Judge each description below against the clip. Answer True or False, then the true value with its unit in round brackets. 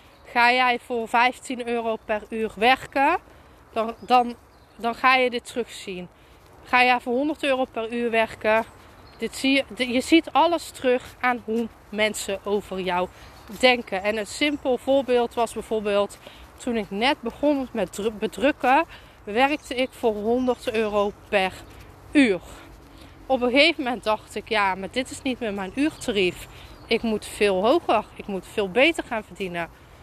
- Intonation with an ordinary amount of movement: True (3.5 semitones)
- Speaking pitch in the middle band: False (235 Hz)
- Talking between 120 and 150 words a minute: False (160 wpm)